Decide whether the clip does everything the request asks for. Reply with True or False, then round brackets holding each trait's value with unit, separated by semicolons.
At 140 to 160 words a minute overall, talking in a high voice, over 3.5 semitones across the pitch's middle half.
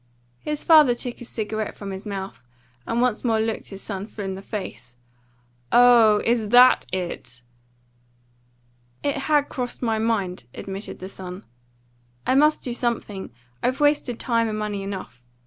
True (155 wpm; 220 Hz; 4.0 semitones)